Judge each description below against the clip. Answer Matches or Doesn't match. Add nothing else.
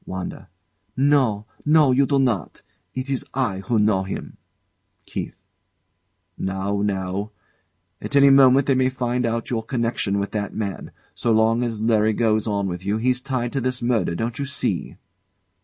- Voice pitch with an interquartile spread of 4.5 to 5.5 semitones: Doesn't match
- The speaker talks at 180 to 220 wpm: Doesn't match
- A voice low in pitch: Matches